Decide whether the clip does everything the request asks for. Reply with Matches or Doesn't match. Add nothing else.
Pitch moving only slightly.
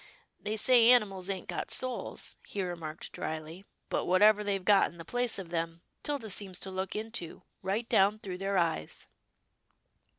Doesn't match